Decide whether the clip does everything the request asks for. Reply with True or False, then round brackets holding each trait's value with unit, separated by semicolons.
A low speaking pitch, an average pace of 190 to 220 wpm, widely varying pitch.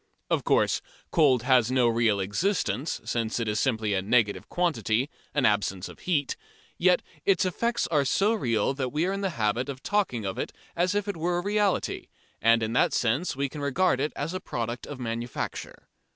True (130 Hz; 195 wpm; 7.4 semitones)